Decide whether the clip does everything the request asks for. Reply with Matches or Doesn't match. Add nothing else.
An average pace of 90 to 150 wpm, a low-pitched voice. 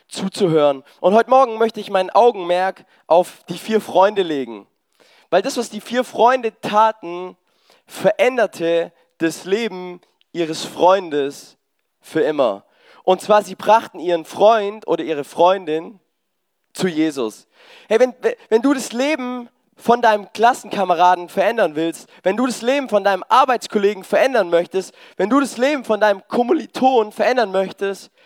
Doesn't match